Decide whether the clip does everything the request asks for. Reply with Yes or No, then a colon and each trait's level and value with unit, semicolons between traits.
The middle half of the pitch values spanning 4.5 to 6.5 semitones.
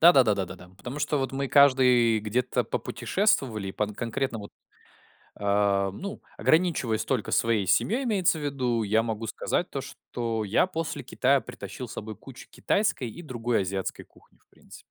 Yes: average, 4.8 semitones